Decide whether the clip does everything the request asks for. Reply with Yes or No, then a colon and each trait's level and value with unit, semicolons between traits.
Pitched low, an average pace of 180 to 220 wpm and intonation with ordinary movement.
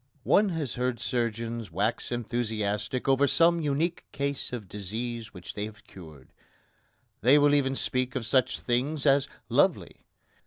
No: low, 125 Hz; average, 145 wpm; average, 4.2 semitones